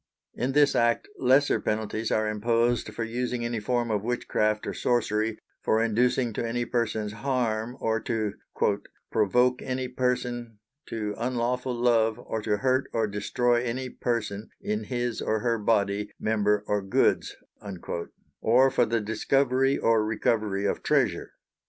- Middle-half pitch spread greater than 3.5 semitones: No, narrow, 2.4 semitones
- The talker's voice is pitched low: Yes, low, 115 Hz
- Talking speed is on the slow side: No, average, 145 wpm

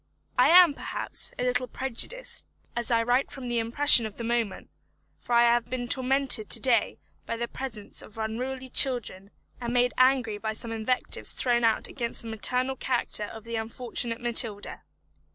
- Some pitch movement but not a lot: No, narrow, 2.0 semitones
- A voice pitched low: No, high, 240 Hz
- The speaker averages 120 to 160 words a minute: No, average, 170 wpm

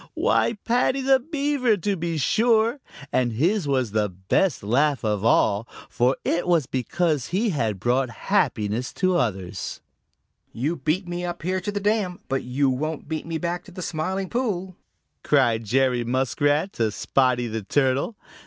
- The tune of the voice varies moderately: No, wide, 7.3 semitones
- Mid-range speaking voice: Yes, medium, 150 Hz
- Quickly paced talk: No, average, 160 wpm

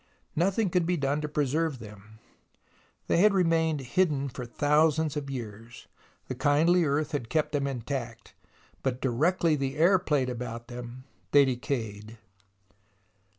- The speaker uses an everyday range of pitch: Yes, average, 4.6 semitones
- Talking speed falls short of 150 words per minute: Yes, average, 140 wpm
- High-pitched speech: No, medium, 140 Hz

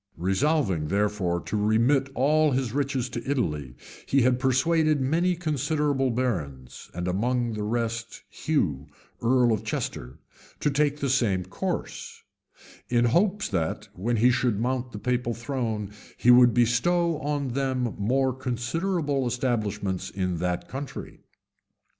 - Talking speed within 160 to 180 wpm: No, slow, 135 wpm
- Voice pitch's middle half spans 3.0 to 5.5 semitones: Yes, average, 4.8 semitones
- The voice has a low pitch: Yes, low, 125 Hz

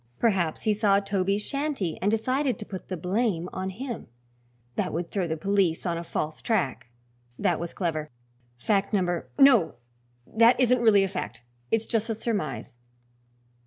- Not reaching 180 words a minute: Yes, average, 160 wpm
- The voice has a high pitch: Yes, high, 200 Hz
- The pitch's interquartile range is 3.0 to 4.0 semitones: No, average, 4.8 semitones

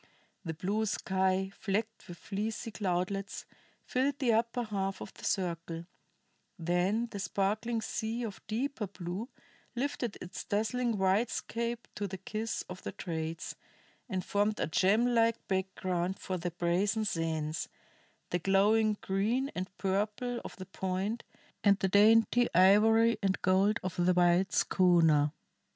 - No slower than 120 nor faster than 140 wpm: Yes, slow, 135 wpm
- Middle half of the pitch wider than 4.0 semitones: No, average, 3.4 semitones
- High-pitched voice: Yes, high, 195 Hz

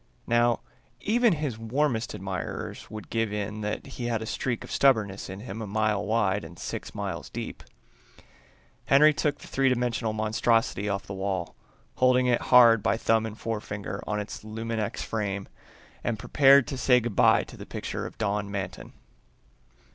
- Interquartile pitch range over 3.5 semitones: No, average, 3.2 semitones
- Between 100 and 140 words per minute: No, average, 170 wpm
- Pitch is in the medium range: No, low, 110 Hz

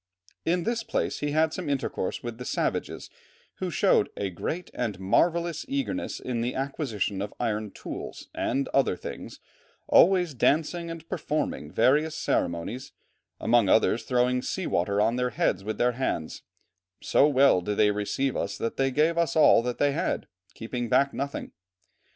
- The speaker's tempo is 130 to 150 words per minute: No, average, 160 wpm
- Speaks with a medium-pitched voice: No, low, 130 Hz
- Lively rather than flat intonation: Yes, wide, 6.3 semitones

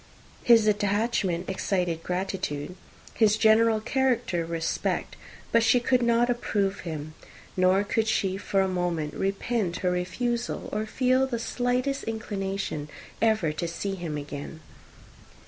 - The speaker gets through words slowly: Yes, slow, 130 wpm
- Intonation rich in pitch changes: No, average, 4.5 semitones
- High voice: Yes, high, 200 Hz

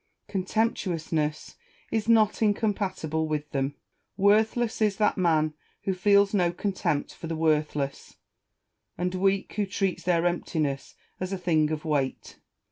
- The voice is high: No, medium, 180 Hz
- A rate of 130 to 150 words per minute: Yes, slow, 135 wpm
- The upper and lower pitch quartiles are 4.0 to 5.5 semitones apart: Yes, average, 4.5 semitones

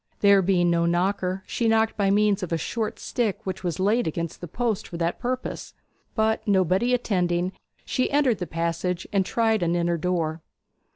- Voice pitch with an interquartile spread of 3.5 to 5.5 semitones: Yes, average, 4.2 semitones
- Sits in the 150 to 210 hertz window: Yes, high, 190 Hz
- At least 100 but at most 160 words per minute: No, average, 180 wpm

